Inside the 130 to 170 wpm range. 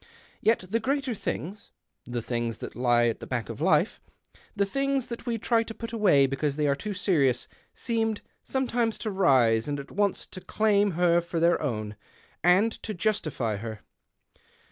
No: average, 190 wpm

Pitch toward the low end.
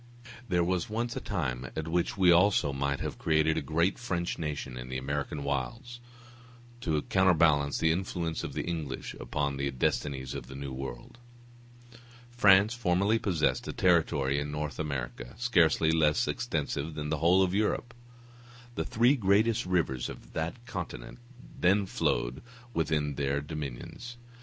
Yes: very low, 80 Hz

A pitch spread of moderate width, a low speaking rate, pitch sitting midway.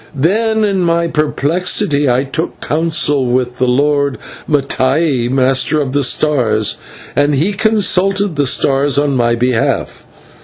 Yes: average, 4.4 semitones; slow, 130 wpm; medium, 145 Hz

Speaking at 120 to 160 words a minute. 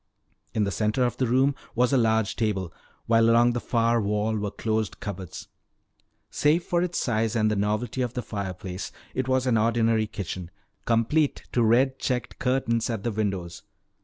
No: average, 175 wpm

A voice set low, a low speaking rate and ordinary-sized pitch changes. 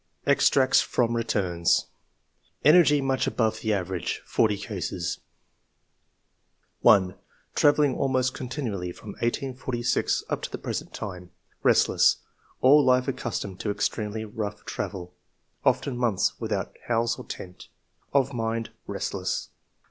Yes: low, 115 Hz; slow, 125 wpm; average, 4.6 semitones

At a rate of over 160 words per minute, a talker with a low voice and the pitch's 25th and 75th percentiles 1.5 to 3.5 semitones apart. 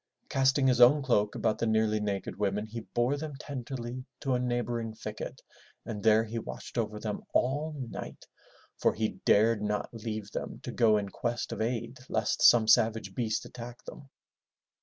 Yes: average, 175 wpm; low, 115 Hz; narrow, 2.6 semitones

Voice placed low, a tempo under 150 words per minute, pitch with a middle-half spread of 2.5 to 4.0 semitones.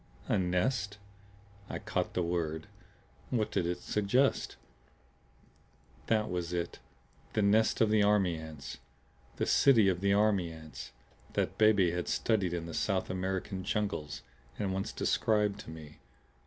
Yes: very low, 95 Hz; average, 140 wpm; average, 3.5 semitones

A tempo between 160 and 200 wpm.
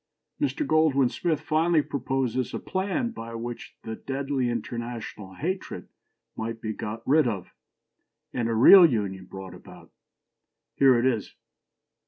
No: average, 140 wpm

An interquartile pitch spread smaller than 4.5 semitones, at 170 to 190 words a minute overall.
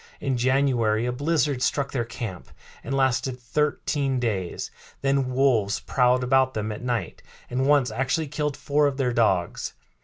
No: average, 2.7 semitones; average, 155 wpm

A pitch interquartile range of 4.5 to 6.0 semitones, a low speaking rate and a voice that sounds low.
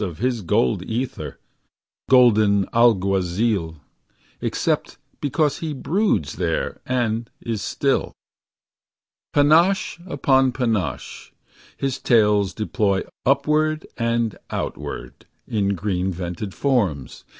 Yes: average, 5.3 semitones; slow, 95 wpm; low, 115 Hz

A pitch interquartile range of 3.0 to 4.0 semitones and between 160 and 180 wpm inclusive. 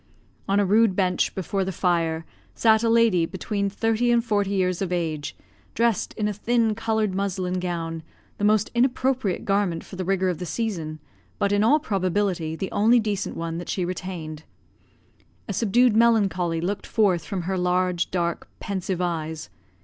Yes: average, 3.5 semitones; average, 170 wpm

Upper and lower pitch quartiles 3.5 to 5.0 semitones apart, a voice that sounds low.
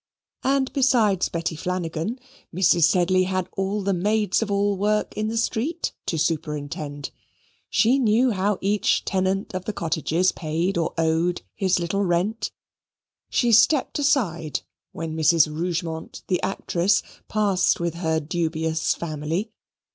No: average, 4.2 semitones; medium, 185 Hz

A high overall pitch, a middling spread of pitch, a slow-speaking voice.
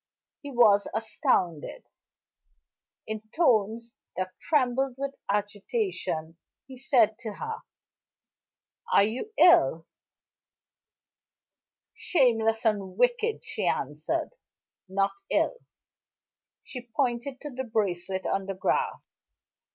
Yes: high, 225 Hz; average, 5.0 semitones; slow, 95 wpm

